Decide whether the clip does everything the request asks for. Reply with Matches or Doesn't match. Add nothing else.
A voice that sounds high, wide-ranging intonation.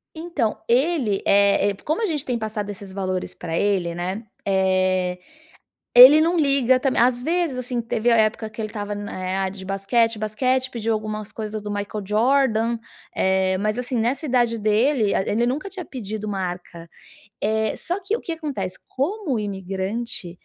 Doesn't match